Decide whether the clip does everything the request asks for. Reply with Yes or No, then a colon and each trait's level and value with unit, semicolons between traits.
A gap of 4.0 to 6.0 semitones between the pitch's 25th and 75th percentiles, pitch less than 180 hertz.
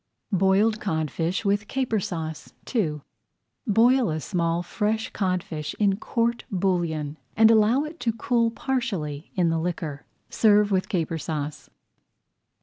No: wide, 5.4 semitones; high, 190 Hz